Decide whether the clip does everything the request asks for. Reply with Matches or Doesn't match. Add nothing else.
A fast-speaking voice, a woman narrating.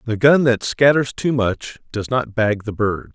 Doesn't match